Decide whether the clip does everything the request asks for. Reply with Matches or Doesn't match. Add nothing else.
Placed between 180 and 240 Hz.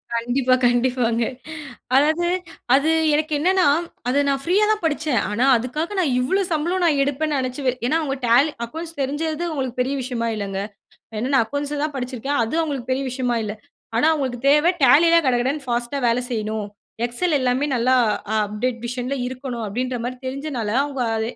Doesn't match